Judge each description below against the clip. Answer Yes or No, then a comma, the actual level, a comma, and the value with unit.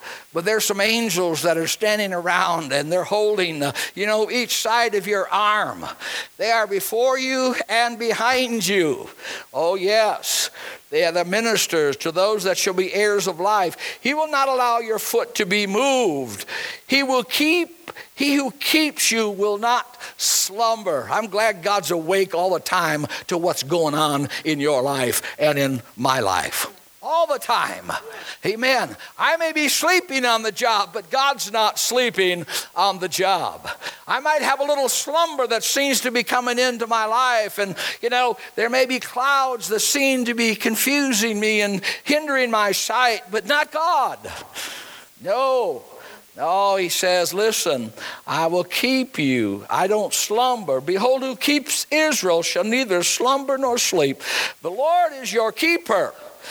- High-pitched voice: Yes, high, 225 Hz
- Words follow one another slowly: No, average, 165 wpm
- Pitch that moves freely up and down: Yes, wide, 5.7 semitones